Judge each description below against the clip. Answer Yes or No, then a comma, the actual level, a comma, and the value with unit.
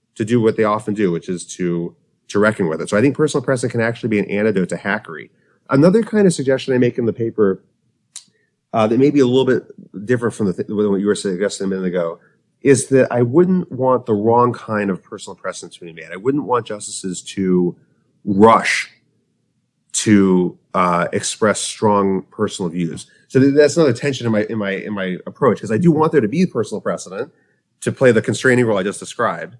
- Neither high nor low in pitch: No, low, 115 Hz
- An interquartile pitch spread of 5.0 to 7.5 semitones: No, average, 4.4 semitones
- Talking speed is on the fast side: Yes, fast, 215 wpm